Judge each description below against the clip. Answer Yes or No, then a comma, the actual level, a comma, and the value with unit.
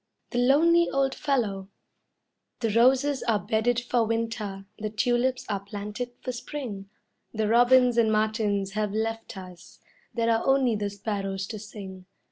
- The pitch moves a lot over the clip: No, average, 3.3 semitones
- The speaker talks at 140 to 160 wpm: Yes, average, 145 wpm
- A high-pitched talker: Yes, high, 225 Hz